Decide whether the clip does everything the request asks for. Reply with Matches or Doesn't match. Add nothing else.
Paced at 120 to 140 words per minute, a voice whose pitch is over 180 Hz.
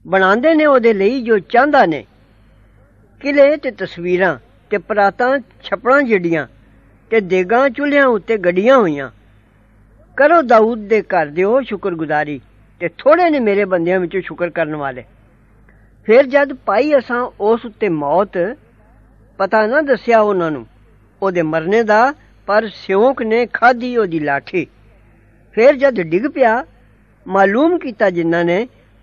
Matches